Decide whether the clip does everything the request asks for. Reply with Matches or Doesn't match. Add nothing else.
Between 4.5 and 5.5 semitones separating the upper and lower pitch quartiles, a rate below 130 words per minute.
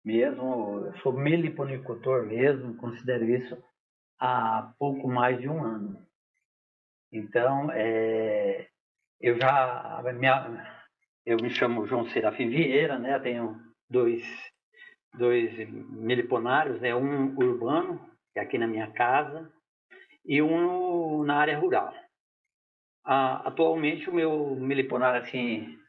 Matches